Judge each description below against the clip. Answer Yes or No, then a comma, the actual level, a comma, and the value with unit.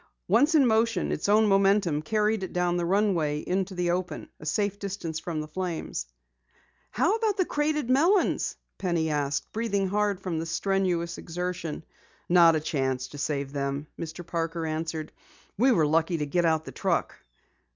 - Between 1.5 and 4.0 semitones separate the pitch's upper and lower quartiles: No, average, 4.4 semitones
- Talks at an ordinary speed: Yes, average, 170 wpm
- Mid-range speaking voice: Yes, medium, 175 Hz